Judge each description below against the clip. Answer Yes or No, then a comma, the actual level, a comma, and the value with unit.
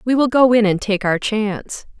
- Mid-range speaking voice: No, high, 220 Hz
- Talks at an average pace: No, fast, 240 wpm